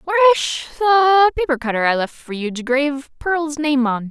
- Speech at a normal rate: Yes, average, 190 wpm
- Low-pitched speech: No, very high, 295 Hz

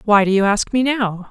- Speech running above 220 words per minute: Yes, fast, 275 wpm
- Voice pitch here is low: No, high, 215 Hz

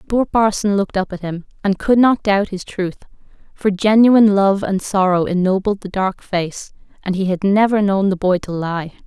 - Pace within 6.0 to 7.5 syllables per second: No, 5.0 syllables/s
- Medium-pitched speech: No, high, 195 Hz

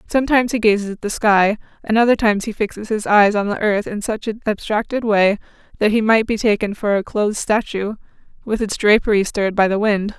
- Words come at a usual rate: No, fast, 220 wpm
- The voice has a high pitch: Yes, high, 210 Hz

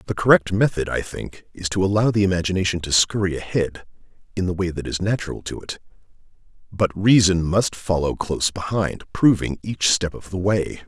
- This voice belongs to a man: Yes, male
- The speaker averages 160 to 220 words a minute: Yes, average, 180 wpm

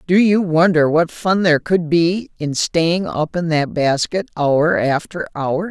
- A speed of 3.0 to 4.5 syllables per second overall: Yes, 4.0 syllables/s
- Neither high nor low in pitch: Yes, medium, 165 Hz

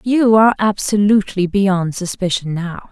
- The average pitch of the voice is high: Yes, high, 195 Hz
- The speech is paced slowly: Yes, slow, 125 wpm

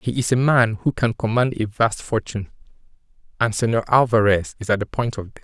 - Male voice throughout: Yes, male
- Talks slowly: No, average, 200 wpm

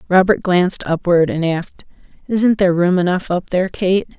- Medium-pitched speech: Yes, medium, 180 Hz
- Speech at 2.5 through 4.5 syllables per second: No, 5.4 syllables/s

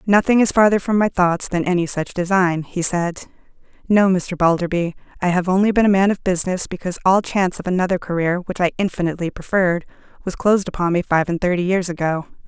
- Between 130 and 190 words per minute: No, average, 200 wpm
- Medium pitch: Yes, medium, 180 Hz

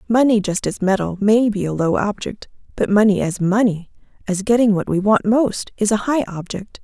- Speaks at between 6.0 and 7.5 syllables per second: No, 5.1 syllables/s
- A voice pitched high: Yes, high, 205 Hz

